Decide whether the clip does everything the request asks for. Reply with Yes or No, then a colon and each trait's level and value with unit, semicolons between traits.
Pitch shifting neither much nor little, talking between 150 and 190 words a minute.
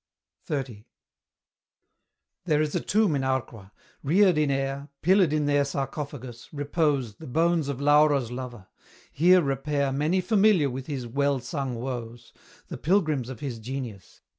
No: average, 3.2 semitones; average, 140 wpm